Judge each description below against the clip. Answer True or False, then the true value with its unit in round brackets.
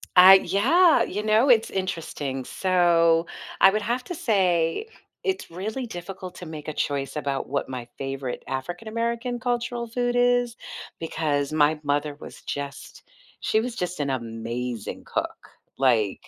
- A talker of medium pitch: True (175 Hz)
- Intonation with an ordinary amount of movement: False (8.3 semitones)